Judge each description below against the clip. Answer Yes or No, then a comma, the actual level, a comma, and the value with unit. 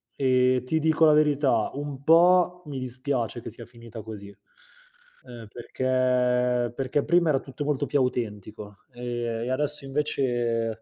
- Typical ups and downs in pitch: Yes, average, 3.4 semitones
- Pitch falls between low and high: No, low, 130 Hz